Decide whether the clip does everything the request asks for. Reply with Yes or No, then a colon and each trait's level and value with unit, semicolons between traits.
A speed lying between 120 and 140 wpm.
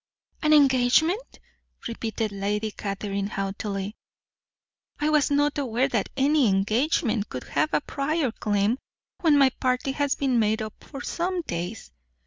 Yes: slow, 135 wpm